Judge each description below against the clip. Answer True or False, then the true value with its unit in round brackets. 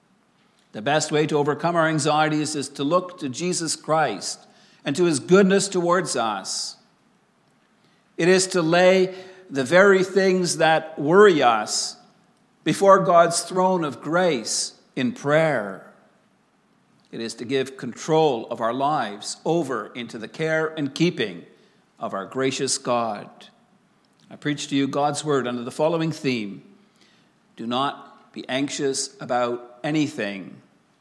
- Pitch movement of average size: True (4.6 semitones)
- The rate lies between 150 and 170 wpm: False (135 wpm)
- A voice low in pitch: False (155 Hz)